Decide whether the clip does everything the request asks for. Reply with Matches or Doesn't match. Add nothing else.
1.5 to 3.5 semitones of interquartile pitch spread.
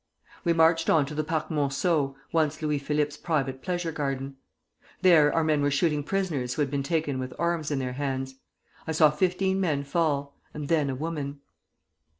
Matches